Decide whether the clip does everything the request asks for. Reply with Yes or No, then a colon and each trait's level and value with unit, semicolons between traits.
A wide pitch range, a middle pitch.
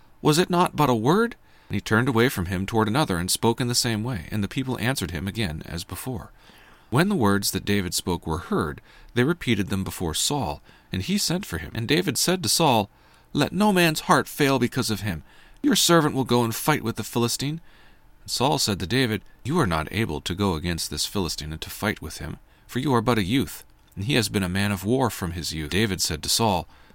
No: wide, 5.7 semitones; low, 110 Hz